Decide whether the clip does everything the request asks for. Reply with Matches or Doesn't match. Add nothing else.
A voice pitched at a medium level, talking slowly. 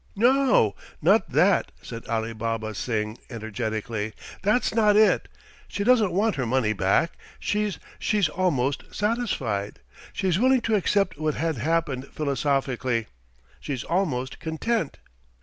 Matches